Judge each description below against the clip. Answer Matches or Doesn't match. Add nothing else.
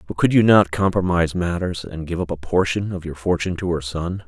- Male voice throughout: Matches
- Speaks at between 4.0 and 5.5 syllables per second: Doesn't match